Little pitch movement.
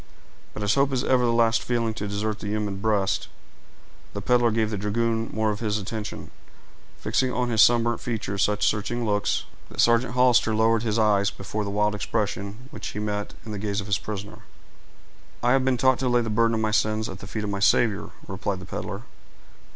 Yes: narrow, 2.2 semitones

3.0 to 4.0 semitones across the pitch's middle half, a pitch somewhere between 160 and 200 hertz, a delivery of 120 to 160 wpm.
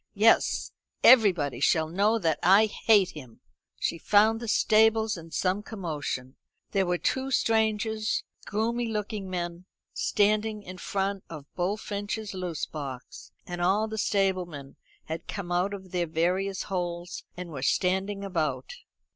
Yes: average, 3.6 semitones; high, 190 Hz; average, 140 wpm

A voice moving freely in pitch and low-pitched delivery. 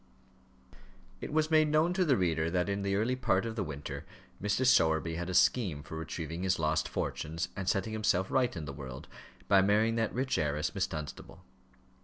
Yes: wide, 6.0 semitones; very low, 95 Hz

